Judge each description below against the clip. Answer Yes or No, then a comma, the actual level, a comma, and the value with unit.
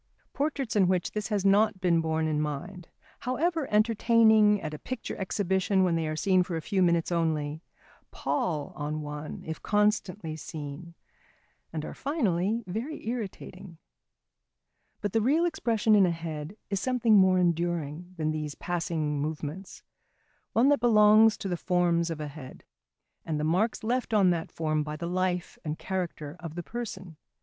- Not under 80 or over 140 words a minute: No, average, 165 wpm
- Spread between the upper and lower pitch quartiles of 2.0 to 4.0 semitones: No, average, 5.0 semitones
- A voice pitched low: No, medium, 180 Hz